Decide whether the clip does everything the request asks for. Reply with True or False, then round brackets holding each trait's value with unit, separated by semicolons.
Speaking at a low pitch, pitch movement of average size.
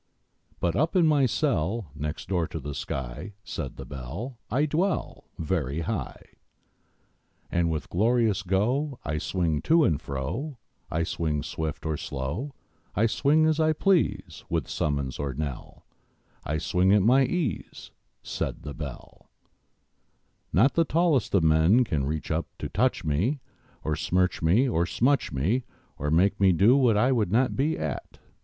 False (95 Hz; 9.0 semitones)